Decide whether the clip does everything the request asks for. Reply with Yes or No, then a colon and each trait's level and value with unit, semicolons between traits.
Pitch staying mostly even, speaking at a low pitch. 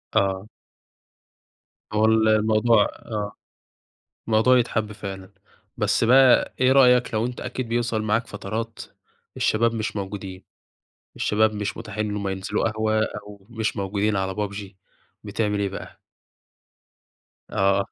Yes: narrow, 2.1 semitones; low, 110 Hz